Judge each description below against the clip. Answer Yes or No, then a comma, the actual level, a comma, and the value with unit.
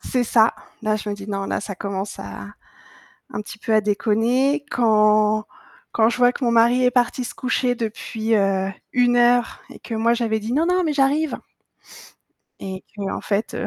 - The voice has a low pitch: No, high, 225 Hz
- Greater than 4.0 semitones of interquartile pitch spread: No, average, 2.8 semitones